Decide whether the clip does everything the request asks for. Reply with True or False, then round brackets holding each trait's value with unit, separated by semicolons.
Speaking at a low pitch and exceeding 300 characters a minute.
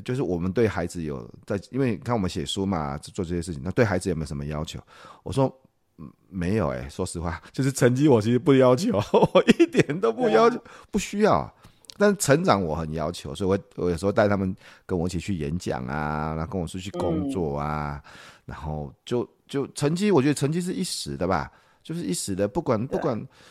True (95 Hz; 310 characters per minute)